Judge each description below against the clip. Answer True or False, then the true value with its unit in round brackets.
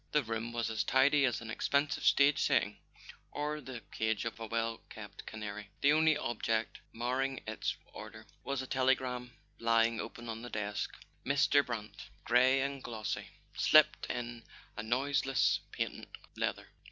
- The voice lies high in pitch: False (120 Hz)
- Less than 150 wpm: False (155 wpm)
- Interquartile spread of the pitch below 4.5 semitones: True (3.3 semitones)